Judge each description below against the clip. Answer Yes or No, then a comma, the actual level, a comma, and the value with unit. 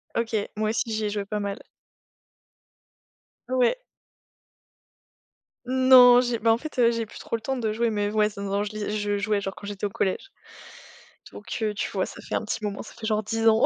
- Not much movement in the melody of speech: Yes, narrow, 2.2 semitones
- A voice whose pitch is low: No, high, 215 Hz